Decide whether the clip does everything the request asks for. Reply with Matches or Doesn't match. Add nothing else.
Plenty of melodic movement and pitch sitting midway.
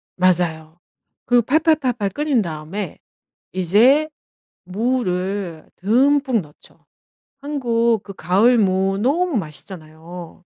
Doesn't match